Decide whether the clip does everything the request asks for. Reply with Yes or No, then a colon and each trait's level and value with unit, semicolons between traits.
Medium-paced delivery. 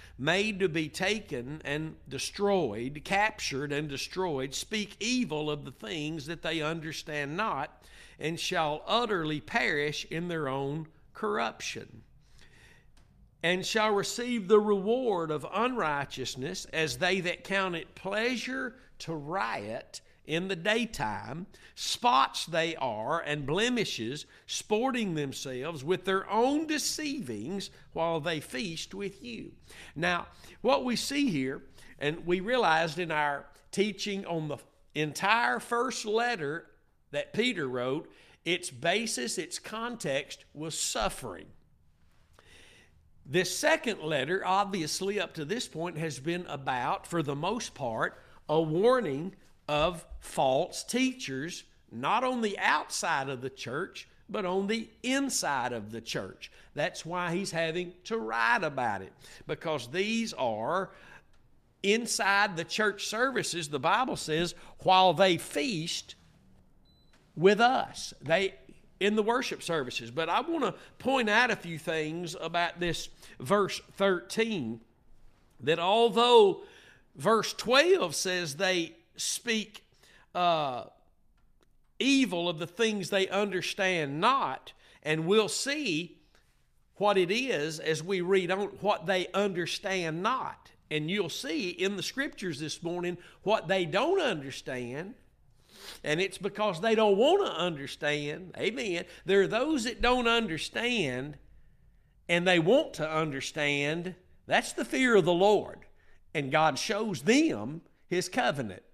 No: slow, 130 wpm